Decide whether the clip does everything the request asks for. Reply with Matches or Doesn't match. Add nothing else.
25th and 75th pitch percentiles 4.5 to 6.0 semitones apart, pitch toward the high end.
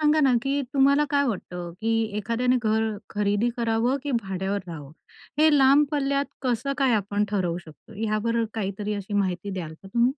Matches